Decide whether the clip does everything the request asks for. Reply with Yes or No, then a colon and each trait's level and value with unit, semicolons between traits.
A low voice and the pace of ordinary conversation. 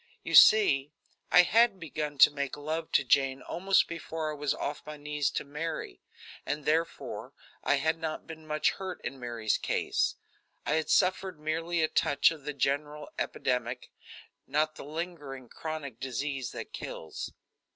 No: medium, 150 Hz; average, 160 wpm